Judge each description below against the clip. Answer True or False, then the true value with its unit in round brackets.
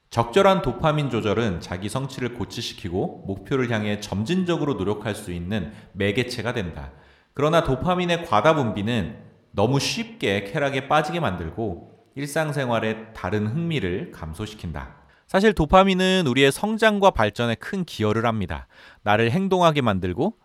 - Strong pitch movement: True (7.3 semitones)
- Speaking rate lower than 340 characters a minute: True (330 characters per minute)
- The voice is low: True (115 Hz)